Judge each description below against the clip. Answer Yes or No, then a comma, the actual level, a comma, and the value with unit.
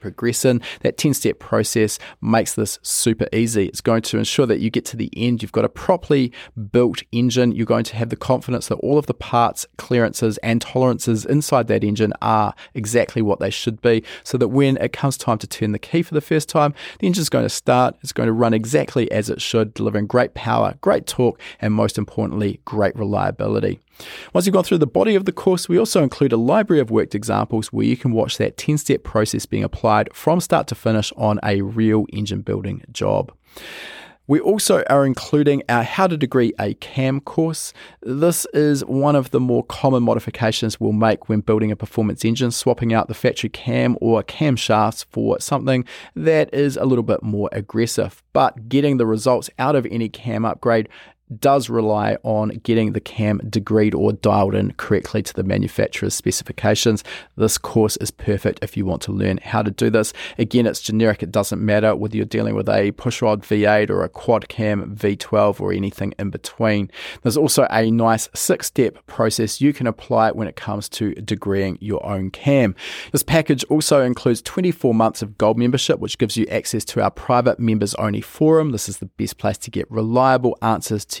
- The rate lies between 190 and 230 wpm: Yes, average, 200 wpm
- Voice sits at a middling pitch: No, low, 115 Hz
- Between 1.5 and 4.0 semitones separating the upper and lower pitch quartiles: Yes, average, 3.4 semitones